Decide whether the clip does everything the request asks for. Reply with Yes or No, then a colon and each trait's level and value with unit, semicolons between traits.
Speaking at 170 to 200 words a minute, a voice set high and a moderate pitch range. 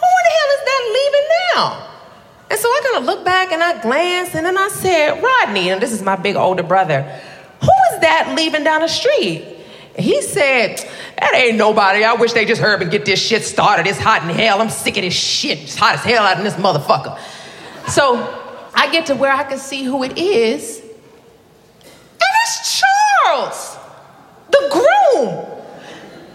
No: average, 195 wpm; very high, 320 Hz; wide, 8.4 semitones